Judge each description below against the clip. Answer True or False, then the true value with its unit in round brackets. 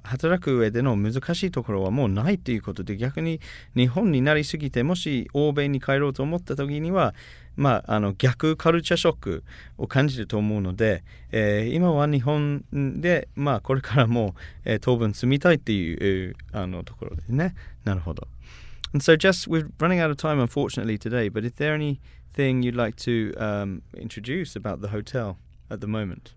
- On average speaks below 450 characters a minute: False (505 characters per minute)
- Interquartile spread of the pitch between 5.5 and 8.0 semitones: True (5.8 semitones)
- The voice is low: True (125 Hz)